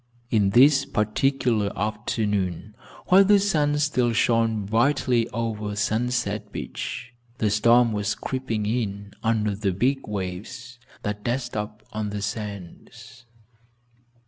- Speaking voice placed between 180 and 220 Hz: No, low, 110 Hz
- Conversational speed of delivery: No, slow, 120 wpm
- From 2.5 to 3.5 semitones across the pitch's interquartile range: Yes, average, 3.1 semitones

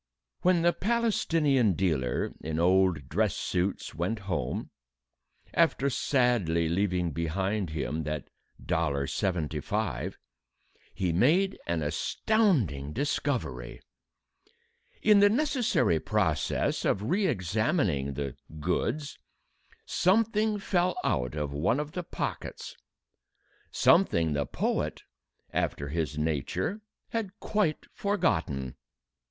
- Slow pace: Yes, slow, 100 wpm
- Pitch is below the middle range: Yes, very low, 95 Hz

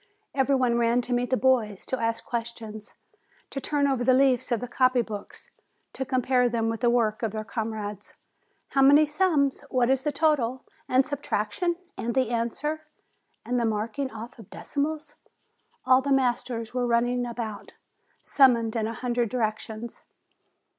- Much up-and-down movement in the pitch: No, average, 2.7 semitones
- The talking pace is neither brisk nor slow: Yes, average, 170 wpm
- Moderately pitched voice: No, high, 245 Hz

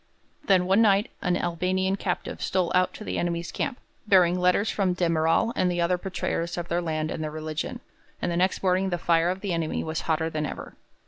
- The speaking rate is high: Yes, fast, 215 wpm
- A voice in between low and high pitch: Yes, medium, 175 Hz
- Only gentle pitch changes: Yes, narrow, 2.0 semitones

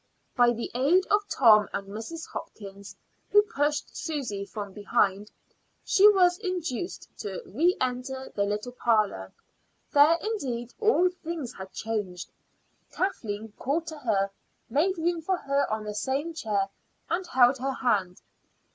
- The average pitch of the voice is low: No, very high, 255 Hz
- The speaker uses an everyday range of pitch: No, wide, 7.9 semitones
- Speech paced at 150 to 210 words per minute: No, average, 140 wpm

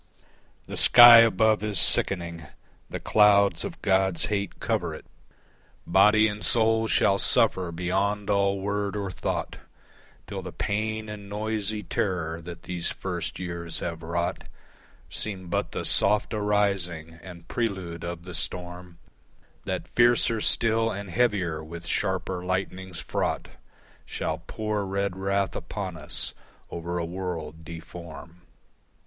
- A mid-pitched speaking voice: No, very low, 95 Hz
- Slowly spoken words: Yes, slow, 130 wpm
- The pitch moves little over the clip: No, average, 3.4 semitones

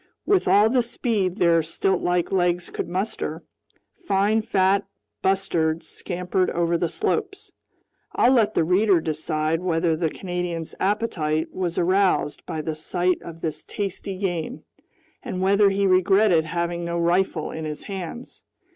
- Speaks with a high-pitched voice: No, medium, 180 Hz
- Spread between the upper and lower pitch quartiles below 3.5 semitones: Yes, average, 3.0 semitones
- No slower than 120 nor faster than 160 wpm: Yes, average, 140 wpm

